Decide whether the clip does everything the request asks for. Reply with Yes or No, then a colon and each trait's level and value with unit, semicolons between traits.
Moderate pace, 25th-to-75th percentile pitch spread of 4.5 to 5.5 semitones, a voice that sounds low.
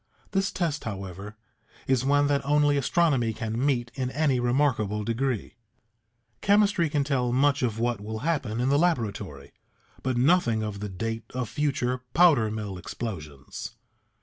Yes: average, 150 wpm; average, 4.9 semitones; low, 125 Hz